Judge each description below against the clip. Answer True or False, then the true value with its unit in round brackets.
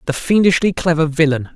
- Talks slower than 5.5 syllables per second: False (5.8 syllables/s)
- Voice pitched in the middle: True (160 Hz)